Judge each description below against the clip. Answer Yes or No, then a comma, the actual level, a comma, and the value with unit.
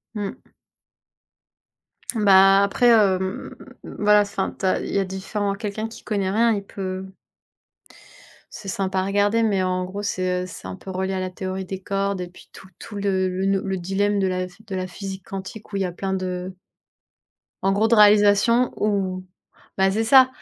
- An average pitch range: No, narrow, 1.6 semitones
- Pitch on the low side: No, high, 195 Hz